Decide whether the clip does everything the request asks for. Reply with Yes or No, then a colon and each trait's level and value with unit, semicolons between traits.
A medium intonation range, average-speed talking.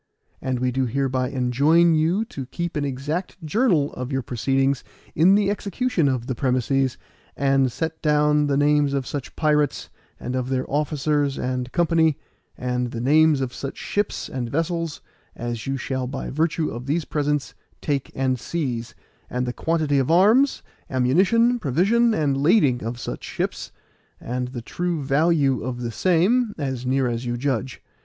Yes: average, 4.1 semitones; average, 165 wpm